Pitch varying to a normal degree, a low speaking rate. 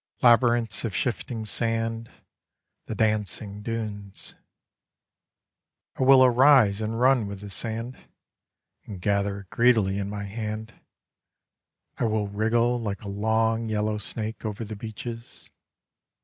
No: narrow, 2.2 semitones; slow, 120 wpm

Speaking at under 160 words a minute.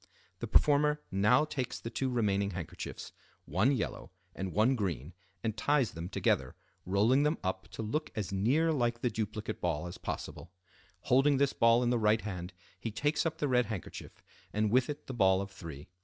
No: average, 185 wpm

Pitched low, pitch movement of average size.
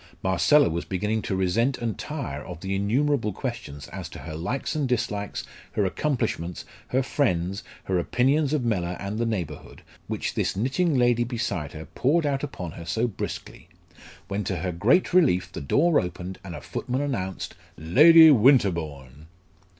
No: low, 105 Hz; wide, 7.0 semitones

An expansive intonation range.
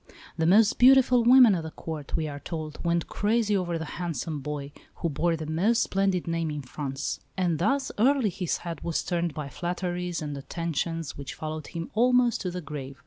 No: average, 4.1 semitones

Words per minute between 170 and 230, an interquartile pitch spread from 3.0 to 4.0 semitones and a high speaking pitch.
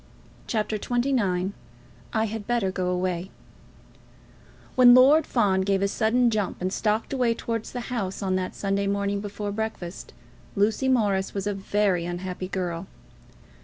No: average, 145 wpm; average, 3.3 semitones; high, 200 Hz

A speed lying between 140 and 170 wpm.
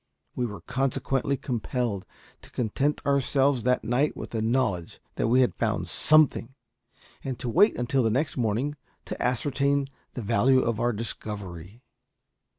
Yes: average, 150 wpm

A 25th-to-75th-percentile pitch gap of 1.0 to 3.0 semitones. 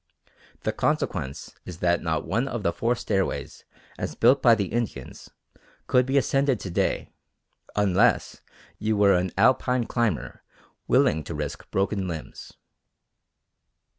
No: average, 5.2 semitones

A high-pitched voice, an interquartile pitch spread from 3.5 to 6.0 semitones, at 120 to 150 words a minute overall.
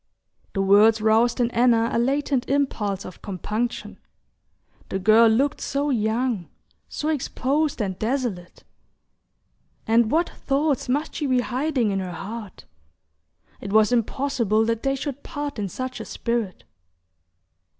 Yes: high, 235 Hz; average, 4.2 semitones; slow, 135 wpm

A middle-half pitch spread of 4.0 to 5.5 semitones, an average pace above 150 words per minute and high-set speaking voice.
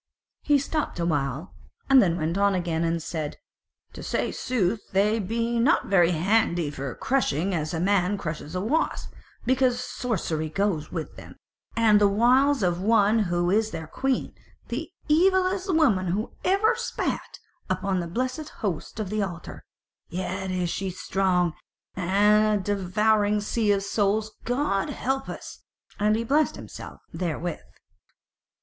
No: average, 4.8 semitones; average, 145 wpm; high, 200 Hz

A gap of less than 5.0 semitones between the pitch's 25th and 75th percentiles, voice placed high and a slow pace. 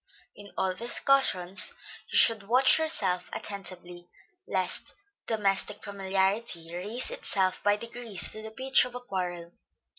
Yes: average, 4.0 semitones; high, 200 Hz; slow, 125 wpm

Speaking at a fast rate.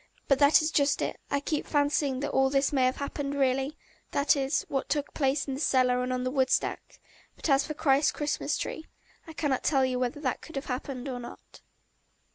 Yes: fast, 215 wpm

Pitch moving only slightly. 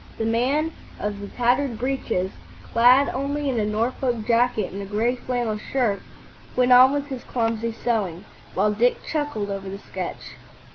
No: average, 3.4 semitones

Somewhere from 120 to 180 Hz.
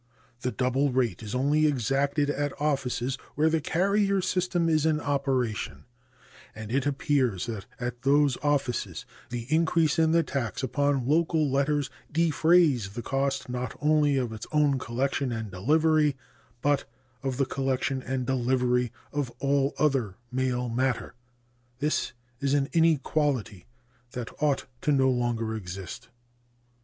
Yes: low, 135 Hz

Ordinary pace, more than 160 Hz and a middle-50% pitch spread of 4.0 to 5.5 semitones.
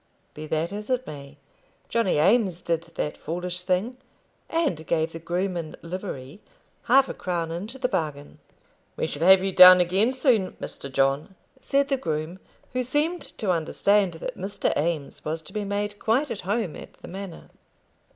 Yes: average, 170 wpm; medium, 185 Hz; average, 4.9 semitones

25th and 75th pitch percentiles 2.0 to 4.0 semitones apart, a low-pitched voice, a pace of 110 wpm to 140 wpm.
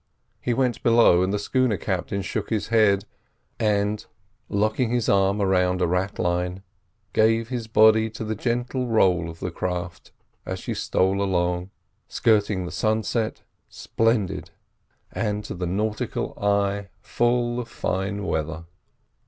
Yes: average, 3.4 semitones; low, 100 Hz; slow, 135 wpm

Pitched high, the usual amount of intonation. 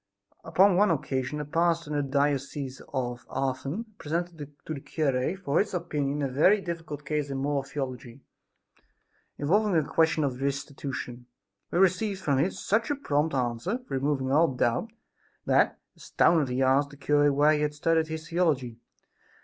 No: medium, 145 Hz; average, 3.5 semitones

